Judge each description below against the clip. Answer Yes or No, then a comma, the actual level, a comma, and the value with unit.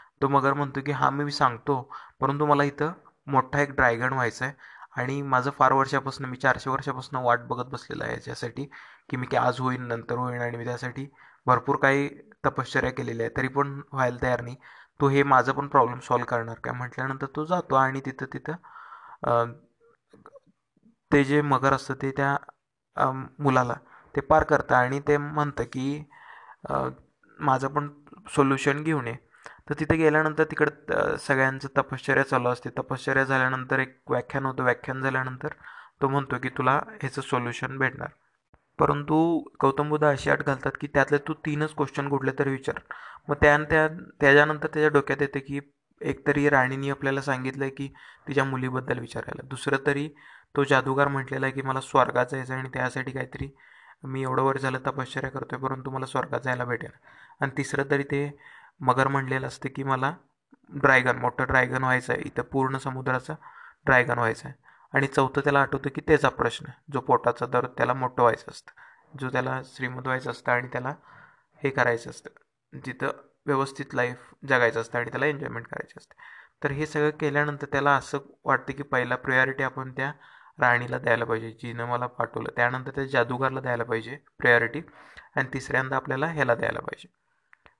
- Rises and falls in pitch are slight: Yes, narrow, 2.0 semitones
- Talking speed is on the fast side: Yes, fast, 165 wpm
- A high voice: No, low, 135 Hz